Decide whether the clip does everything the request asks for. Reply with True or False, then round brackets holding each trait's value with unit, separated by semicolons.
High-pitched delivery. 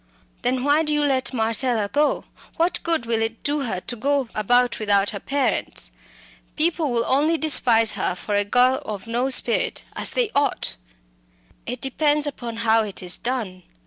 True (250 Hz)